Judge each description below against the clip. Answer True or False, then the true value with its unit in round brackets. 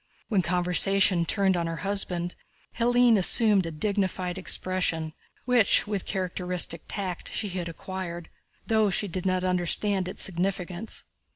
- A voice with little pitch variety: True (2.3 semitones)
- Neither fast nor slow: False (130 wpm)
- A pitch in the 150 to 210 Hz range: True (185 Hz)